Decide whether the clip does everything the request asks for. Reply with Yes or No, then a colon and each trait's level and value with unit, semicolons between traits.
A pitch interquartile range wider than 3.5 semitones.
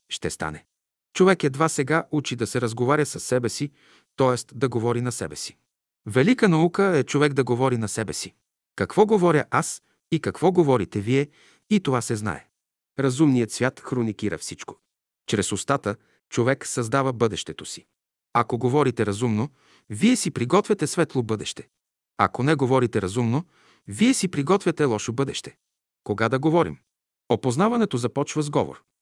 Yes: average, 4.7 semitones